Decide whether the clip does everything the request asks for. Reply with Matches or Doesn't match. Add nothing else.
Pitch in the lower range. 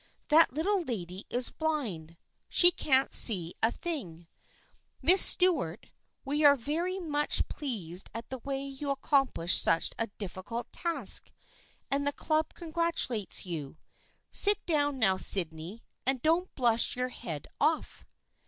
Doesn't match